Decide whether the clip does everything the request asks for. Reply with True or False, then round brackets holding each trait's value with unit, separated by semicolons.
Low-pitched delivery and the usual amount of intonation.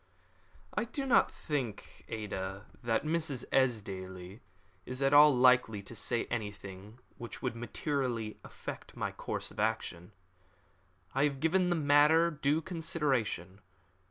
False (125 Hz; 6.0 semitones)